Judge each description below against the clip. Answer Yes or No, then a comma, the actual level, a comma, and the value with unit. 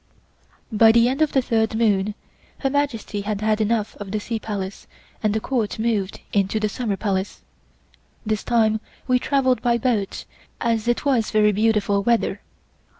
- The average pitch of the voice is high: Yes, high, 220 Hz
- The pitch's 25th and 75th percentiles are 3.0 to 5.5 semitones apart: No, narrow, 2.4 semitones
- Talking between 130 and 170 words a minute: Yes, average, 165 wpm